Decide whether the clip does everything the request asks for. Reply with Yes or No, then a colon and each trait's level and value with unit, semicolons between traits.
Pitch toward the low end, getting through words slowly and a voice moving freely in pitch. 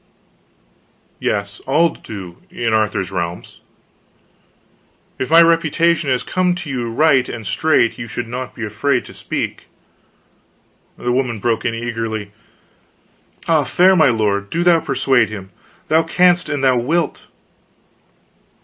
Yes: low, 125 Hz; slow, 130 wpm; wide, 6.5 semitones